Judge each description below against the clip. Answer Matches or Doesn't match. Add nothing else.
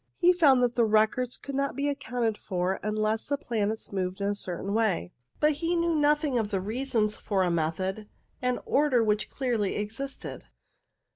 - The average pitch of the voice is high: Matches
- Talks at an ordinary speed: Matches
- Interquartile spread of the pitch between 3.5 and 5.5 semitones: Matches